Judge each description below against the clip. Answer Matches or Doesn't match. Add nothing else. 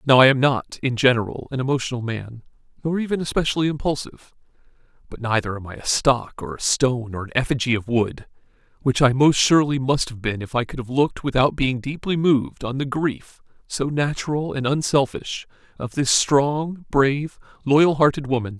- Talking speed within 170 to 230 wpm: Matches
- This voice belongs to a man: Matches